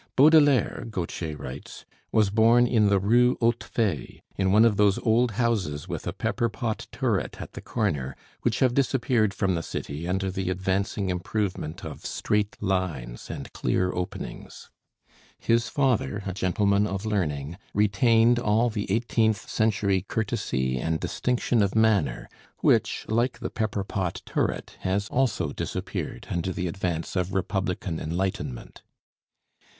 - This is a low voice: Yes, low, 100 Hz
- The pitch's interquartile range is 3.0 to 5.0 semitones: Yes, average, 3.9 semitones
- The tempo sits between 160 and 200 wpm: No, average, 140 wpm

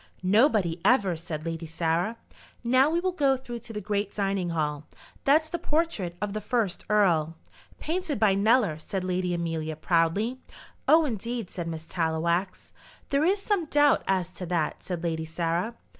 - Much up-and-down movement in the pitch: Yes, wide, 6.8 semitones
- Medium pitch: No, high, 195 Hz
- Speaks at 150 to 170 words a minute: Yes, average, 165 wpm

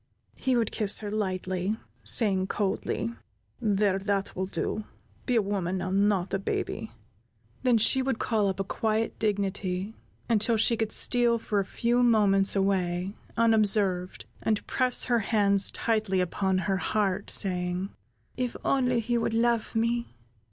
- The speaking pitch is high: Yes, high, 205 Hz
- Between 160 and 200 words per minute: No, average, 150 wpm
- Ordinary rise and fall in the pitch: Yes, average, 3.0 semitones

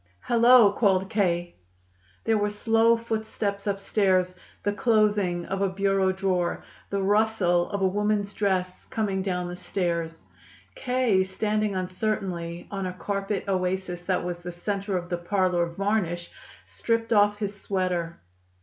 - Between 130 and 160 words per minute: Yes, average, 140 wpm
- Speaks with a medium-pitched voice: No, high, 195 Hz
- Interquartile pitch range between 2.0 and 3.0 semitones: Yes, narrow, 2.4 semitones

